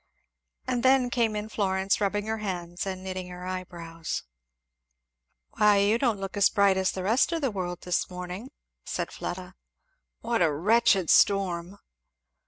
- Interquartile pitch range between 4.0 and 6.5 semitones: No, average, 3.0 semitones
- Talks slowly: No, average, 155 wpm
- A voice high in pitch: Yes, high, 195 Hz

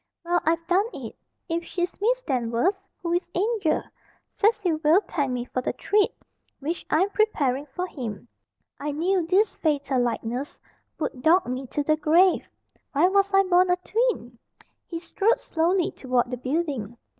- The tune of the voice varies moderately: No, wide, 5.9 semitones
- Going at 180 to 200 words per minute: No, average, 160 wpm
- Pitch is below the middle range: No, very high, 330 Hz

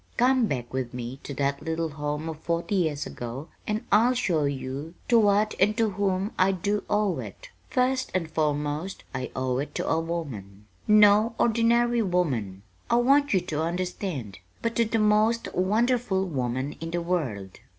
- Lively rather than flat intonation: Yes, wide, 7.0 semitones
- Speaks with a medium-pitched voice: Yes, medium, 175 Hz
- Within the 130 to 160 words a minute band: No, average, 170 wpm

